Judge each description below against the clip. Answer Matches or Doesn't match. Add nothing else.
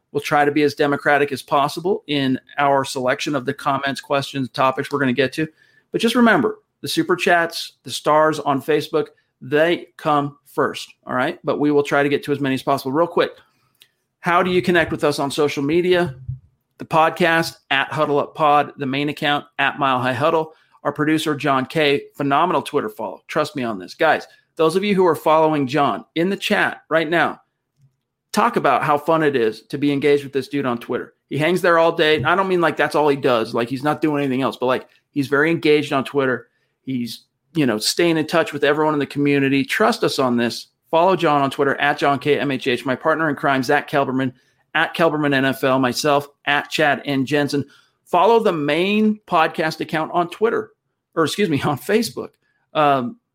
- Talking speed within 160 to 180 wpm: Doesn't match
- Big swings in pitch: Doesn't match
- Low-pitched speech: Doesn't match